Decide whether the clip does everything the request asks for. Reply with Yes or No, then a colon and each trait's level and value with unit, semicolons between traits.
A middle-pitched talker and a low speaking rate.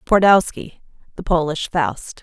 Yes: medium, 175 Hz; slow, 110 wpm